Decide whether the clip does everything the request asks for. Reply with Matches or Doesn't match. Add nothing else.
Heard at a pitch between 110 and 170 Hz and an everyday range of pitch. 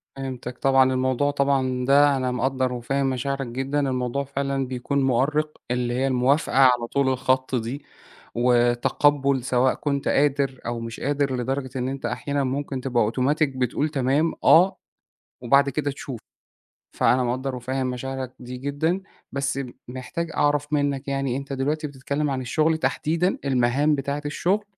Doesn't match